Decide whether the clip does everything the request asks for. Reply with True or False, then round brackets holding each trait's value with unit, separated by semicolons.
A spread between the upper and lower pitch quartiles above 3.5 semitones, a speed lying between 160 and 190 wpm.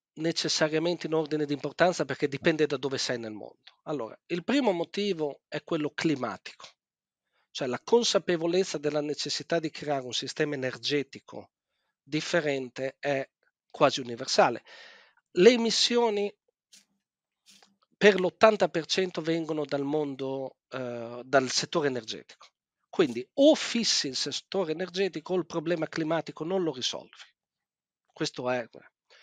False (4.4 semitones; 120 wpm)